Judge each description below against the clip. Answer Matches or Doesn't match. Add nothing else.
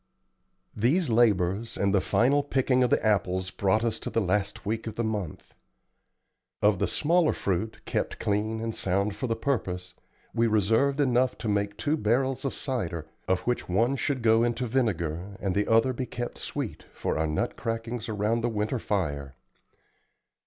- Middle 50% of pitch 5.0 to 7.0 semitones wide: Doesn't match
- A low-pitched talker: Matches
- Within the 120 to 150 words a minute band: Doesn't match